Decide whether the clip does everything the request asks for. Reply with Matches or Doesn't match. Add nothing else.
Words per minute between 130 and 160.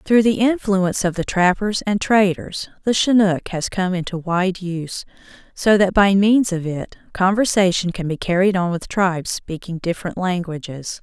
Doesn't match